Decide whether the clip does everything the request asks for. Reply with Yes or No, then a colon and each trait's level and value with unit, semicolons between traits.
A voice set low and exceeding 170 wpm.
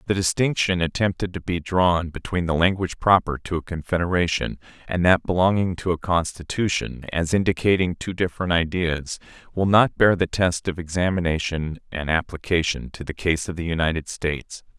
No: very low, 85 Hz; average, 160 wpm